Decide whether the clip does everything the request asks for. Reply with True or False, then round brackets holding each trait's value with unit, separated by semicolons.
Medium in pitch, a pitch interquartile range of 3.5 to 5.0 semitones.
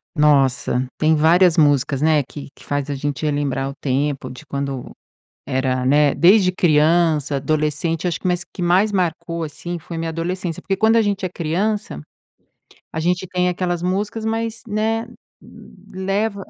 True (165 Hz; 4.4 semitones)